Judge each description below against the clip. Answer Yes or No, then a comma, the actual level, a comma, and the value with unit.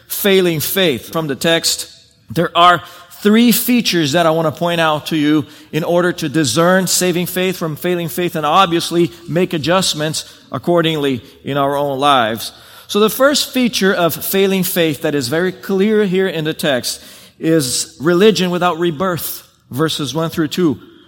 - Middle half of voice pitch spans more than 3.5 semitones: No, average, 3.2 semitones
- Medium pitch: Yes, medium, 170 Hz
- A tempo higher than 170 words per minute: No, average, 165 wpm